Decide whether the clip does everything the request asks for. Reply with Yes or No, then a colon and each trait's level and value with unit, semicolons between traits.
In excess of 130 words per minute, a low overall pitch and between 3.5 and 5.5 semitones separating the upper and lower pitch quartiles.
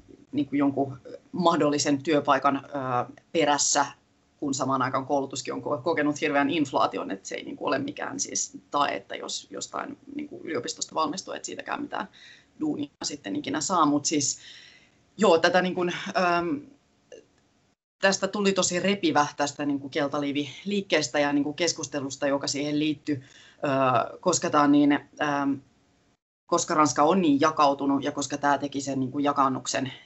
No: average, 150 wpm; medium, 145 Hz; average, 4.0 semitones